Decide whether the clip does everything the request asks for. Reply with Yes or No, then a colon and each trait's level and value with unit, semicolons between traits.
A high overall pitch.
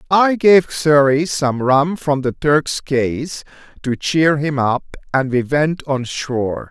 No: medium, 145 Hz